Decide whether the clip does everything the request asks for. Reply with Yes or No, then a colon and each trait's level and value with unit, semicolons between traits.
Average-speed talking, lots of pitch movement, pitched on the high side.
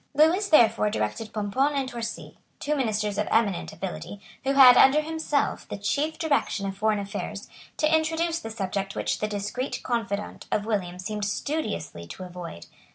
Yes: average, 160 wpm; wide, 6.0 semitones; high, 215 Hz